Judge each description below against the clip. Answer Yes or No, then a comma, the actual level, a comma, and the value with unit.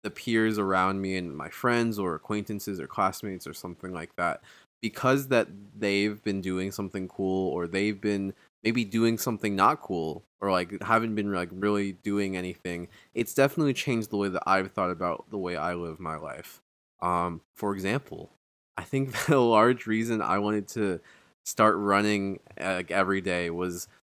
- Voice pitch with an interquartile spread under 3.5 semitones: Yes, average, 2.8 semitones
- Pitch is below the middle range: Yes, low, 100 Hz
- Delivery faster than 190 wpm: No, average, 175 wpm